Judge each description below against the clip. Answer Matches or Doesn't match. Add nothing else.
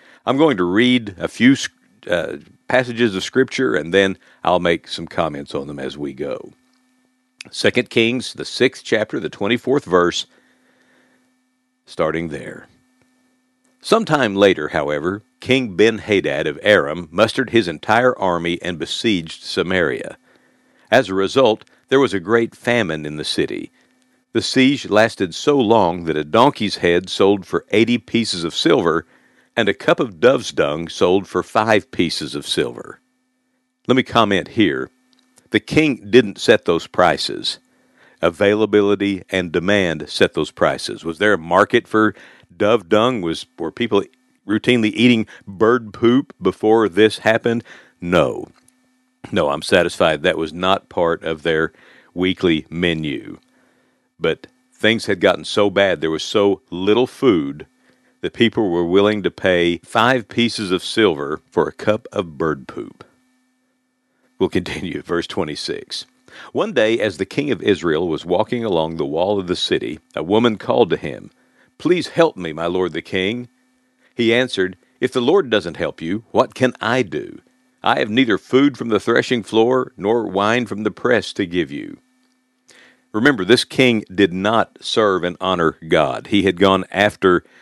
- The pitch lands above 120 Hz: Doesn't match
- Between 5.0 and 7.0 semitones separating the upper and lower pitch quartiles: Matches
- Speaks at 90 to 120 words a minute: Doesn't match